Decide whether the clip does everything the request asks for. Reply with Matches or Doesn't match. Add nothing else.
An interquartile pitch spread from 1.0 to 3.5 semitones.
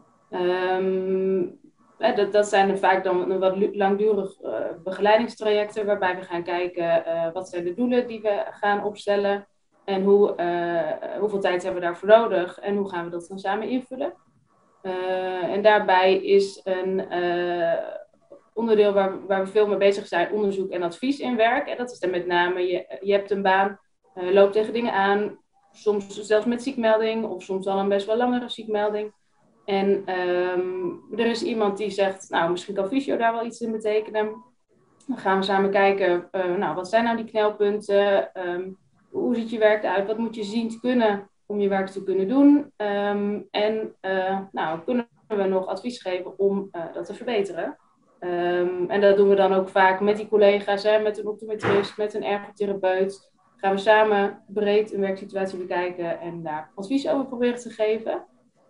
Matches